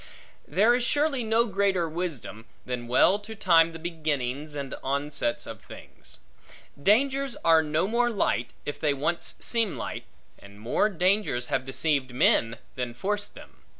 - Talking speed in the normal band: Yes, average, 150 wpm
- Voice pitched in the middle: Yes, medium, 165 Hz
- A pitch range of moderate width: No, wide, 7.7 semitones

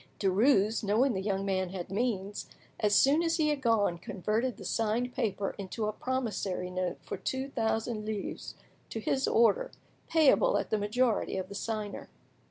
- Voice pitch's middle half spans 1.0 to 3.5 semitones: No, average, 4.2 semitones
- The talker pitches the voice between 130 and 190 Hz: No, high, 215 Hz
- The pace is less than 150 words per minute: No, average, 170 wpm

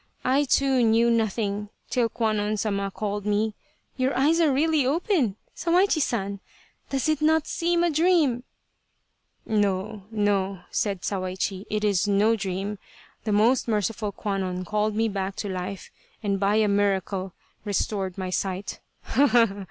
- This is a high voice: Yes, high, 210 Hz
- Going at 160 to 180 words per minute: No, average, 150 wpm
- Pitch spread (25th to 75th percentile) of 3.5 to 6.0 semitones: Yes, average, 4.2 semitones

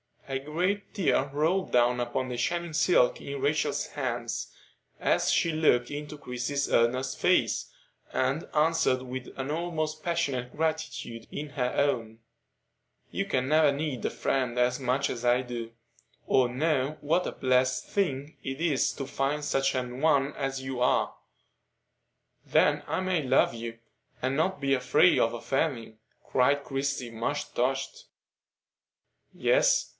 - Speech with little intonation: No, average, 3.7 semitones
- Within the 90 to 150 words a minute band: Yes, average, 145 wpm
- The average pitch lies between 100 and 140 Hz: Yes, low, 135 Hz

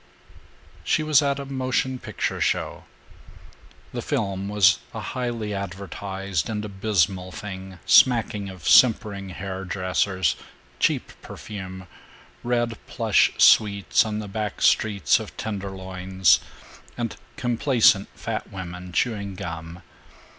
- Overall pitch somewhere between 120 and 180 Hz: No, low, 100 Hz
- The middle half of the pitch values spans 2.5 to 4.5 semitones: Yes, average, 2.9 semitones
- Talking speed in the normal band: No, slow, 115 wpm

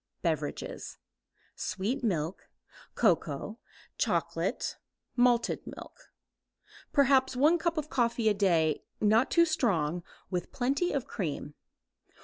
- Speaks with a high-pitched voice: Yes, high, 235 Hz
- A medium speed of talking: No, slow, 105 wpm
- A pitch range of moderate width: No, wide, 7.4 semitones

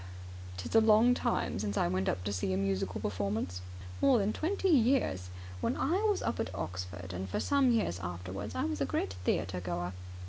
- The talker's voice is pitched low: Yes, very low, 95 Hz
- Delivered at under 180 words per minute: No, average, 195 wpm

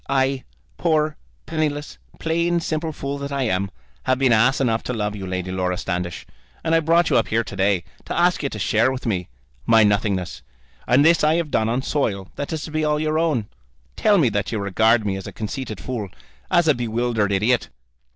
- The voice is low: Yes, low, 125 Hz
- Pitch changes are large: Yes, wide, 6.8 semitones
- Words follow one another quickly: Yes, fast, 210 wpm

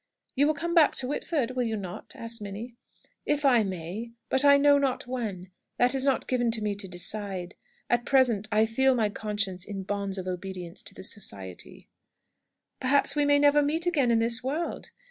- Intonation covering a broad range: Yes, wide, 5.8 semitones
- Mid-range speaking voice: No, high, 230 Hz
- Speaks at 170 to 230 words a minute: Yes, average, 195 wpm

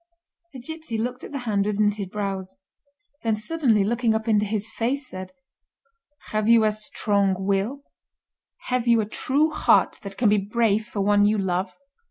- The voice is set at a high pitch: Yes, high, 215 Hz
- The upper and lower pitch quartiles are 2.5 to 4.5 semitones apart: Yes, average, 2.9 semitones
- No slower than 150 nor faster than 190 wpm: Yes, average, 170 wpm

